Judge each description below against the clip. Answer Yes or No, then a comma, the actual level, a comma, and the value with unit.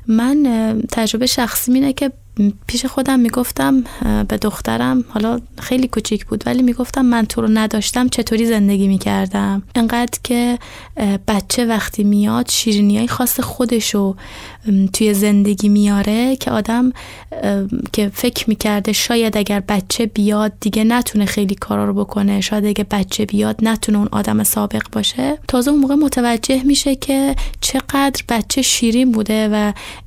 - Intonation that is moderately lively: Yes, average, 3.3 semitones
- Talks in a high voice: Yes, high, 220 Hz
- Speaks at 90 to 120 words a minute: No, average, 140 wpm